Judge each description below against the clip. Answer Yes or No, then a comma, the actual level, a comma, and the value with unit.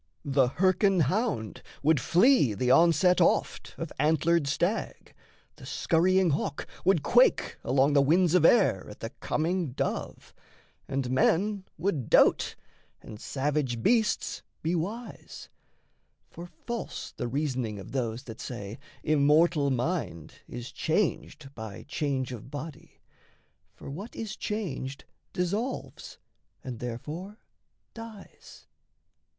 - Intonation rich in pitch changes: Yes, wide, 6.0 semitones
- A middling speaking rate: No, slow, 120 wpm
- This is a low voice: No, medium, 155 Hz